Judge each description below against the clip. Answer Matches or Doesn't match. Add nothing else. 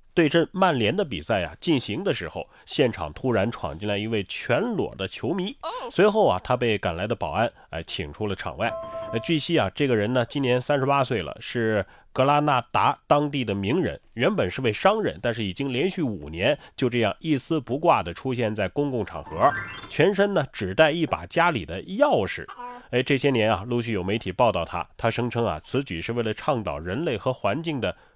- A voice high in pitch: Doesn't match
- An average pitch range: Doesn't match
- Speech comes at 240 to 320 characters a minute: Matches